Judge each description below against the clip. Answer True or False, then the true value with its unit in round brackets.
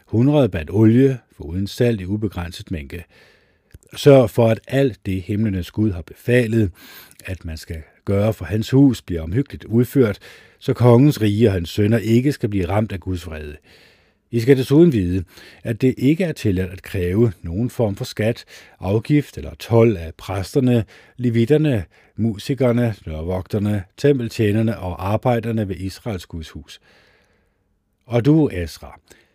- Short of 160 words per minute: True (150 wpm)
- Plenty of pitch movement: False (4.5 semitones)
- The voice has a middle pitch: False (110 Hz)